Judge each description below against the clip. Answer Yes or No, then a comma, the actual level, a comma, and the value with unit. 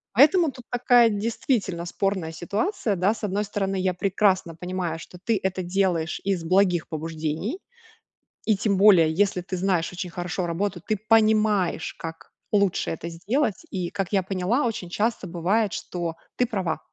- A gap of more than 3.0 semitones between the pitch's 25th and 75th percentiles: Yes, average, 3.4 semitones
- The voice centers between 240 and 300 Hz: No, high, 190 Hz